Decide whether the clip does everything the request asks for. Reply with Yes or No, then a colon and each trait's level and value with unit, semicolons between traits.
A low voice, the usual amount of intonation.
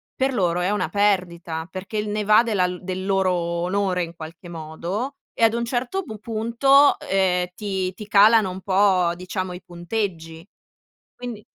No: high, 190 Hz; average, 3.3 semitones